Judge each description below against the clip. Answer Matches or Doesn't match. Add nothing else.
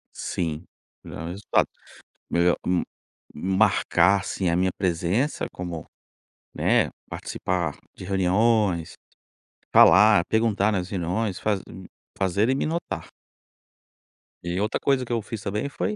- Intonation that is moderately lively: Matches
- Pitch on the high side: Doesn't match